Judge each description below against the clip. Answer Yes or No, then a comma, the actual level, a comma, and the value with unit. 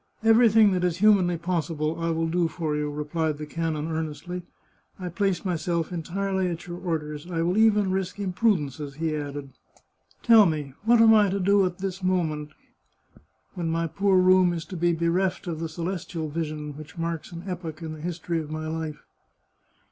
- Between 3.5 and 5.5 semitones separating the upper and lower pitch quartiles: No, average, 2.8 semitones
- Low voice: No, medium, 170 Hz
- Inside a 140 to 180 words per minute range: No, average, 190 wpm